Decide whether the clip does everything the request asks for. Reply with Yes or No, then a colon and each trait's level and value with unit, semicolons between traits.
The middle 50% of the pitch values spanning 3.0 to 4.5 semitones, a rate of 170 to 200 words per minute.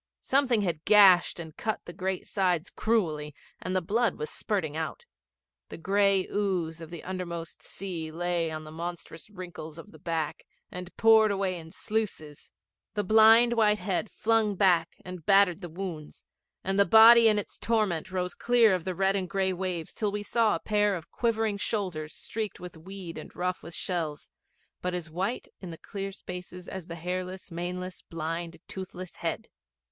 Yes: average, 3.5 semitones; average, 175 wpm